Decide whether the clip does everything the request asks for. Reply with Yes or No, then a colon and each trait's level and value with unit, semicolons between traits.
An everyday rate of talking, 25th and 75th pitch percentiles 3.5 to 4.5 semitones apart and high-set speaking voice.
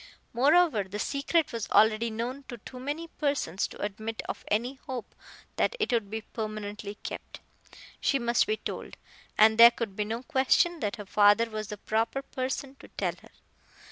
Yes: average, 175 wpm; average, 4.1 semitones; high, 230 Hz